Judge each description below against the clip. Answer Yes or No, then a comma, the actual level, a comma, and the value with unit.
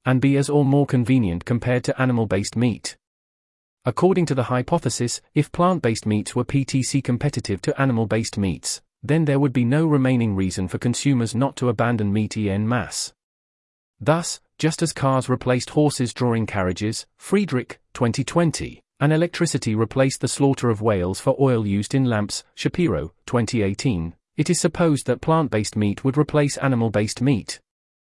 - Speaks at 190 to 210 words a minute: No, average, 165 wpm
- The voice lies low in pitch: Yes, low, 125 Hz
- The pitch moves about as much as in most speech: Yes, average, 4.6 semitones